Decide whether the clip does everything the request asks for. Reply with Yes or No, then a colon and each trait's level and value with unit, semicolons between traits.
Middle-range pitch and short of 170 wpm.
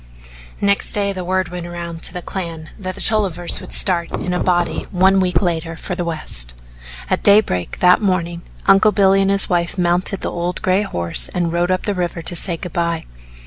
No: medium, 180 Hz; fast, 205 wpm